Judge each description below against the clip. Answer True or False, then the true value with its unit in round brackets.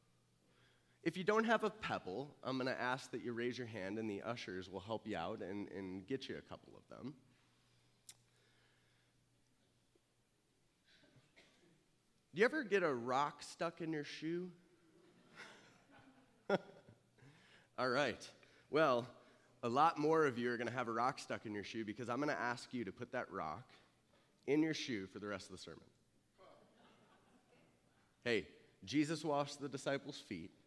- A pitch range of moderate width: False (6.2 semitones)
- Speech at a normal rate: True (160 wpm)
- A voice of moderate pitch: False (125 Hz)